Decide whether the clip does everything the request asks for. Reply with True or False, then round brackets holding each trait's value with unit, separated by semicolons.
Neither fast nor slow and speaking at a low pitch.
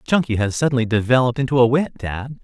True (195 wpm; 125 Hz)